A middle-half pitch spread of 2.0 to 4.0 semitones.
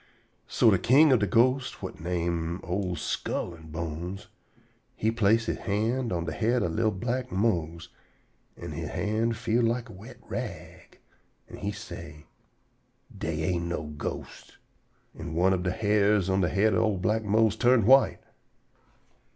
No: average, 4.8 semitones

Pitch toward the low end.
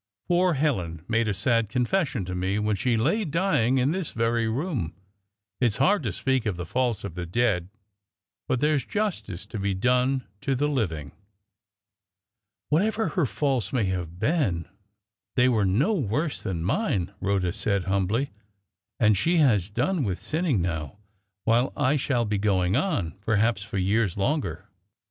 Yes: low, 115 Hz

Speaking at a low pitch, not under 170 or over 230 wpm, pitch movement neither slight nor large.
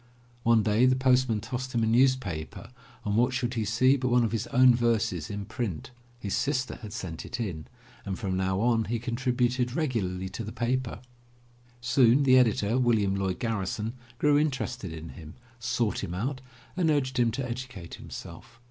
Yes: low, 115 Hz; average, 185 wpm; average, 4.0 semitones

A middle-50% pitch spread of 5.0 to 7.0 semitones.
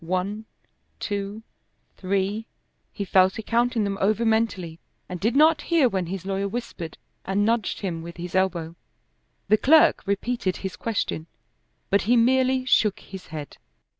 No: average, 3.7 semitones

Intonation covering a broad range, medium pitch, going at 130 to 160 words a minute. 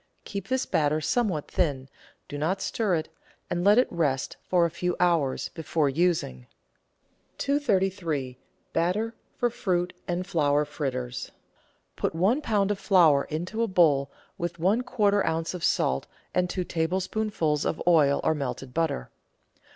No: average, 4.6 semitones; medium, 170 Hz; average, 145 wpm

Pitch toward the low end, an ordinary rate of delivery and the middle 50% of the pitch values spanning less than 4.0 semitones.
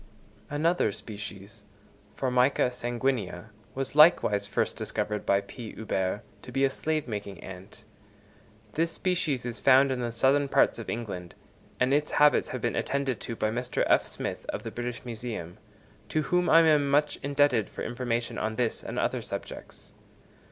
No: low, 125 Hz; average, 160 wpm; average, 4.5 semitones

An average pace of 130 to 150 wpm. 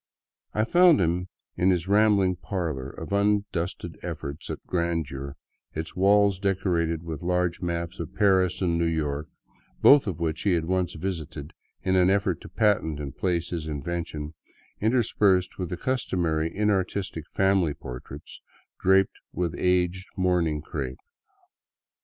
Yes: average, 140 wpm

